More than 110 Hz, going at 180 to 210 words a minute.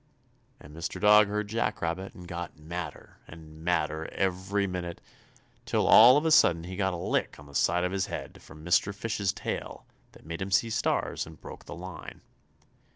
No: very low, 90 Hz; average, 190 wpm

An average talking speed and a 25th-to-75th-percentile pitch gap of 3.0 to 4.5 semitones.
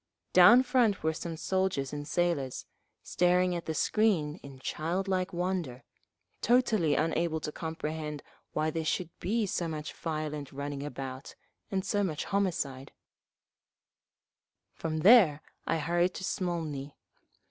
No: slow, 125 wpm; average, 3.7 semitones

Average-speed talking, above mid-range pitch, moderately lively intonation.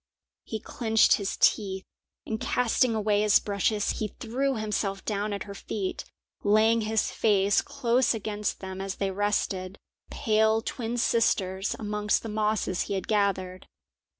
No: average, 145 wpm; high, 210 Hz; narrow, 2.0 semitones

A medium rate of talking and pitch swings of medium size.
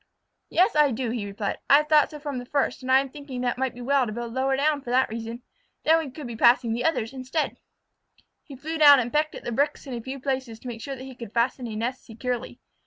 No: fast, 265 wpm; average, 3.1 semitones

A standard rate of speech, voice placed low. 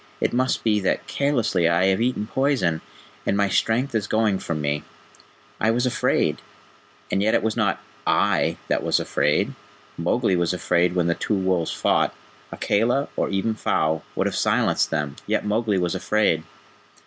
Yes: average, 170 wpm; low, 100 Hz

